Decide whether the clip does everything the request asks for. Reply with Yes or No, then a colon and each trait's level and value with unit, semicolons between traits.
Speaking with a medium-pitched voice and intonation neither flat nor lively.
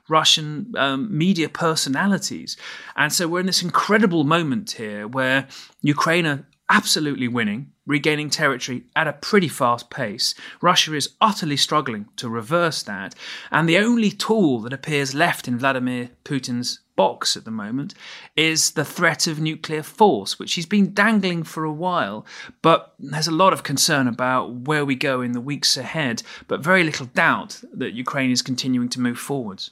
Yes: medium, 155 Hz; average, 4.4 semitones